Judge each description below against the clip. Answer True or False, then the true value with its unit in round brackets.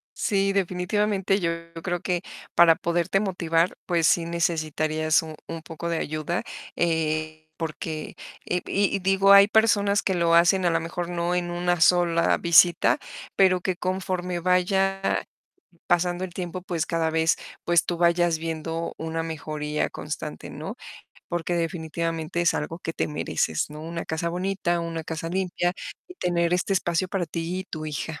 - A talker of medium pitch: True (170 Hz)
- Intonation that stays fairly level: True (1.9 semitones)